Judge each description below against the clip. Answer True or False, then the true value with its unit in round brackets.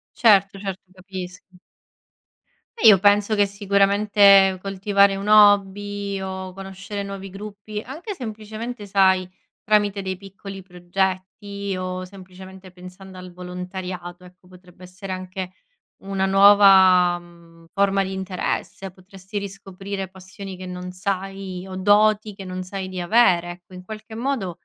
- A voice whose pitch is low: False (195 Hz)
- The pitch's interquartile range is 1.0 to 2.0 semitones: True (1.6 semitones)